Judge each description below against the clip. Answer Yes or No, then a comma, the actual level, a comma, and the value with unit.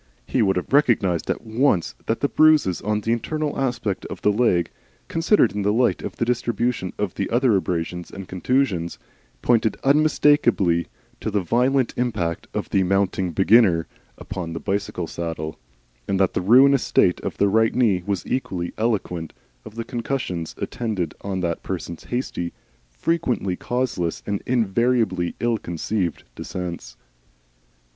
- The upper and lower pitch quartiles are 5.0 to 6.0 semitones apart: Yes, wide, 5.4 semitones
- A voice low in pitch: Yes, low, 105 Hz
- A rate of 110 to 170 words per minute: Yes, average, 150 wpm